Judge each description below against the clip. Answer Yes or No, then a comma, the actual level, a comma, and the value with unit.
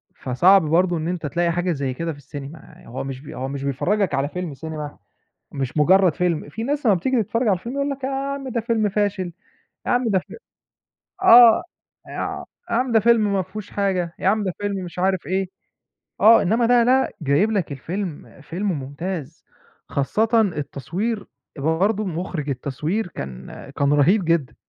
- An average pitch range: No, wide, 6.4 semitones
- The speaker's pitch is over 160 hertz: Yes, medium, 185 Hz